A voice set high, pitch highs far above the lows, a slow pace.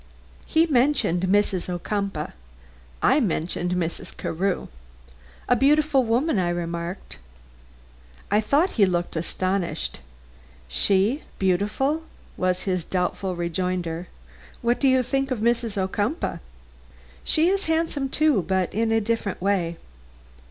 Yes: high, 200 Hz; wide, 6.5 semitones; slow, 115 wpm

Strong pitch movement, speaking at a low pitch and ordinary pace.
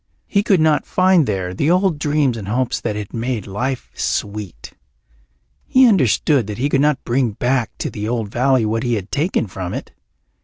Yes: wide, 5.8 semitones; low, 125 Hz; average, 190 wpm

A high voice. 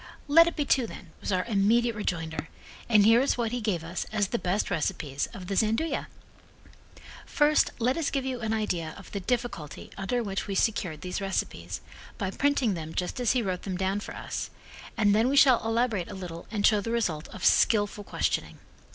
Yes: high, 210 Hz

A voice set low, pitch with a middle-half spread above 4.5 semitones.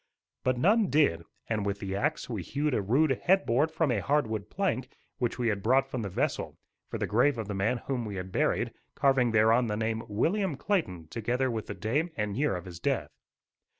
Yes: low, 120 Hz; average, 5.2 semitones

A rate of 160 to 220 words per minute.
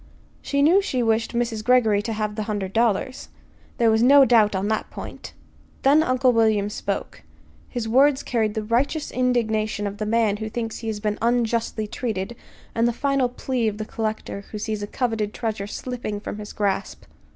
Yes: average, 185 wpm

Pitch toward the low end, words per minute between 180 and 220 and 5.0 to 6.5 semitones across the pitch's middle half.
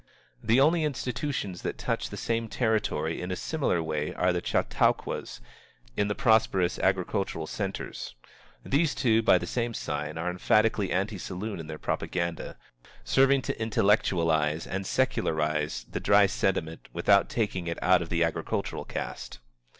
No: very low, 95 Hz; average, 150 wpm; wide, 5.5 semitones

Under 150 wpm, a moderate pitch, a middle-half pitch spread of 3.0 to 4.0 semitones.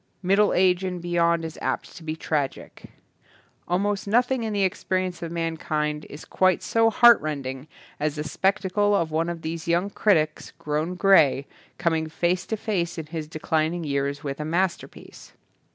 No: average, 170 wpm; medium, 170 Hz; average, 3.5 semitones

